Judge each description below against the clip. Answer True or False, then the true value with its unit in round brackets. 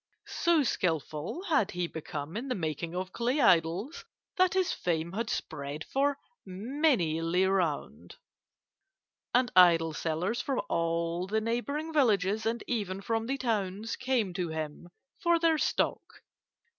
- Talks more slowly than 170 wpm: True (140 wpm)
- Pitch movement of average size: False (7.3 semitones)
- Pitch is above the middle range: True (195 Hz)